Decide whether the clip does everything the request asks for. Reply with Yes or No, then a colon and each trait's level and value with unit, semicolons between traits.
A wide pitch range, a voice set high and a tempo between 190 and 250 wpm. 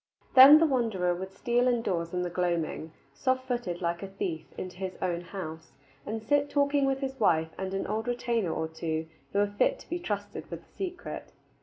Yes: wide, 6.7 semitones; high, 200 Hz; average, 200 wpm